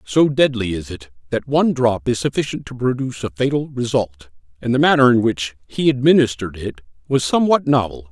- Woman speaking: No, male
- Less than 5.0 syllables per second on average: No, 5.7 syllables/s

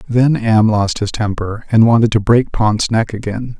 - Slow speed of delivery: No, average, 200 wpm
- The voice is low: Yes, low, 110 Hz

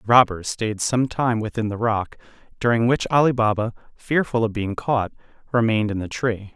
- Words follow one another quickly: No, average, 185 wpm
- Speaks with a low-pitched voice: Yes, low, 115 Hz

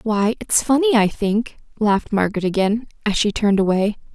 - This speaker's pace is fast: No, average, 175 wpm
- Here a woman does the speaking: Yes, female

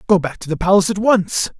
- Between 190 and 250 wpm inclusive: No, fast, 265 wpm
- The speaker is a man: Yes, male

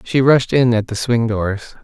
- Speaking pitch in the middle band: No, low, 115 Hz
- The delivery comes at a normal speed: No, fast, 230 wpm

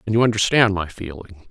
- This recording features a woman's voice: No, male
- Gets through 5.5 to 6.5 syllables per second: Yes, 5.8 syllables/s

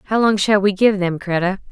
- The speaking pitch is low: No, high, 195 Hz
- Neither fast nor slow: No, fast, 245 wpm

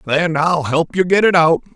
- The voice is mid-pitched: Yes, medium, 165 Hz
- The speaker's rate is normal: No, fast, 240 wpm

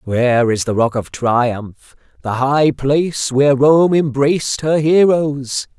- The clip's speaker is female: No, male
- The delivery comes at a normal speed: Yes, average, 145 wpm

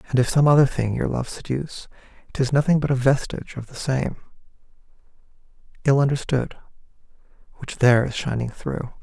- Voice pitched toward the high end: No, low, 135 Hz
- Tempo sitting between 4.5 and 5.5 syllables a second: No, 5.7 syllables/s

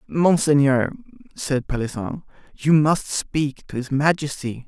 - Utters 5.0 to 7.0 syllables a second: No, 3.9 syllables/s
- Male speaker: Yes, male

